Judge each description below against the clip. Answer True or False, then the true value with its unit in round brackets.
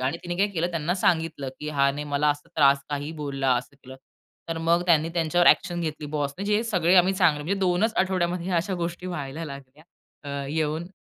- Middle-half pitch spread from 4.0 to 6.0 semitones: False (3.4 semitones)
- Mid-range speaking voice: True (160 Hz)